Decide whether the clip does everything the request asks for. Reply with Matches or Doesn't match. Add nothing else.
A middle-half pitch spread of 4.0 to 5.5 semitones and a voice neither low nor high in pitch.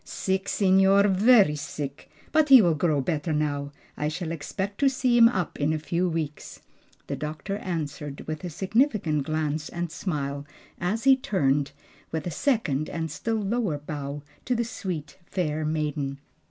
Matches